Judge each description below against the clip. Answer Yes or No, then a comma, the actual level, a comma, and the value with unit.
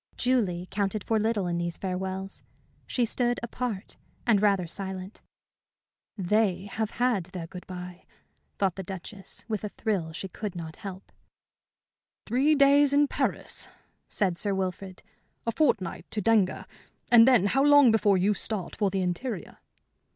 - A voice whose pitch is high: Yes, high, 200 Hz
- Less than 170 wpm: Yes, average, 150 wpm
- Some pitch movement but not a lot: Yes, average, 3.7 semitones